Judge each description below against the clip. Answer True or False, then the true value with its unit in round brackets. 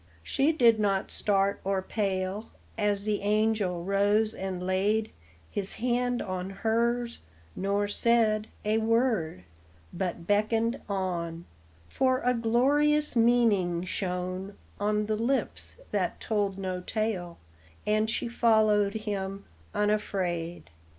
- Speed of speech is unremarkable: False (115 wpm)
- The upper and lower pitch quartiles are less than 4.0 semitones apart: True (3.0 semitones)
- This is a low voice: False (210 Hz)